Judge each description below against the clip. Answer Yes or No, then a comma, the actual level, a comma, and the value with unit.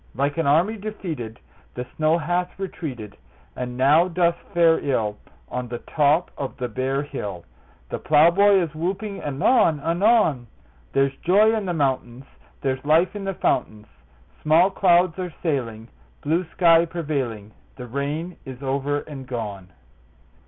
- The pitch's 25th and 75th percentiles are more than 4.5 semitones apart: Yes, average, 5.2 semitones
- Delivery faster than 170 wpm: No, average, 145 wpm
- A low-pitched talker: No, medium, 150 Hz